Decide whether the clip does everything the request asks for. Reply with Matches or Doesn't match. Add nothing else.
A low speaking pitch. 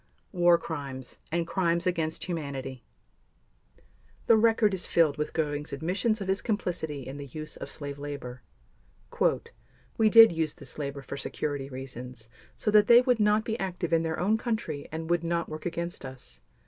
Doesn't match